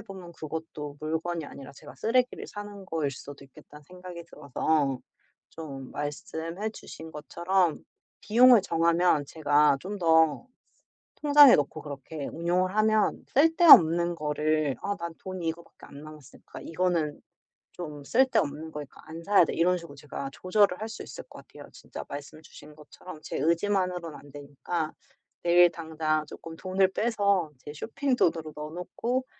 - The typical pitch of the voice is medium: Yes, medium, 165 Hz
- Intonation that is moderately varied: Yes, average, 3.7 semitones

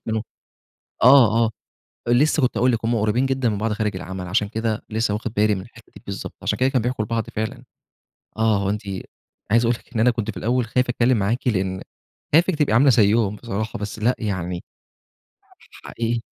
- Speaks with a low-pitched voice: Yes, low, 115 Hz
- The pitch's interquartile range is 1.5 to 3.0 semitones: Yes, average, 2.7 semitones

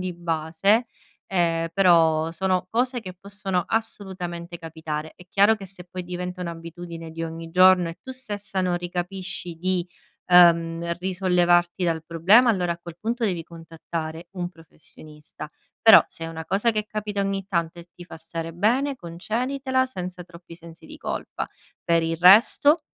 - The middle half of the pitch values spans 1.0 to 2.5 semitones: No, average, 2.9 semitones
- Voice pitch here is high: No, medium, 175 Hz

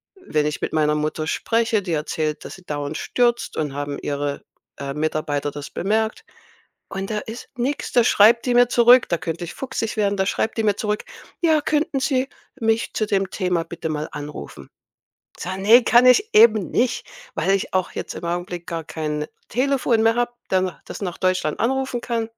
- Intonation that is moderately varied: No, wide, 7.1 semitones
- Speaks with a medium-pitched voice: No, high, 195 Hz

